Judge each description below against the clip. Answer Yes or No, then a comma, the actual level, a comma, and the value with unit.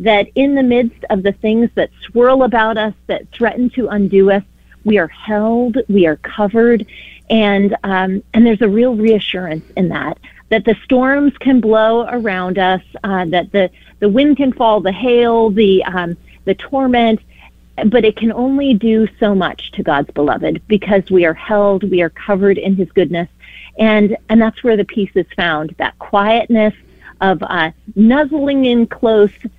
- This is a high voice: Yes, high, 215 Hz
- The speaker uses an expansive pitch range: No, average, 3.3 semitones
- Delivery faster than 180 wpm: No, average, 175 wpm